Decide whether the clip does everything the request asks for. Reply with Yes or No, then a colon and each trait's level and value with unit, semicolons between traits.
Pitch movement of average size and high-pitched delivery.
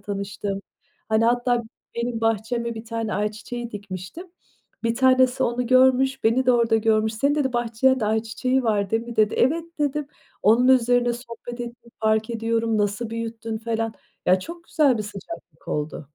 No: narrow, 2.2 semitones; high, 230 Hz